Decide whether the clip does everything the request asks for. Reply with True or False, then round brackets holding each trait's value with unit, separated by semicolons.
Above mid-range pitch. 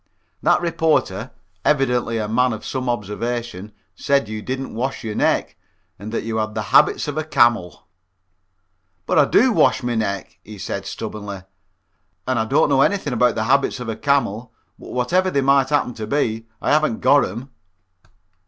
False (120 Hz)